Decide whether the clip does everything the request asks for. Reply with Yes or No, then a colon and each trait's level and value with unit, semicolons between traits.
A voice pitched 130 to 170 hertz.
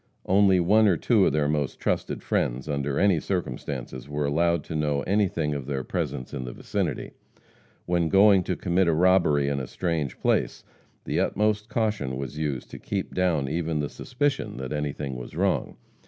No: very low, 75 Hz